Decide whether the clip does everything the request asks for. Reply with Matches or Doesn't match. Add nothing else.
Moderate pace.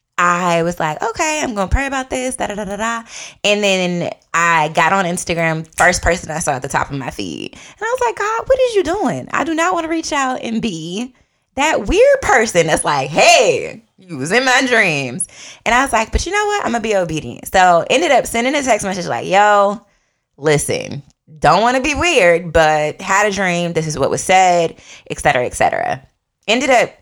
Doesn't match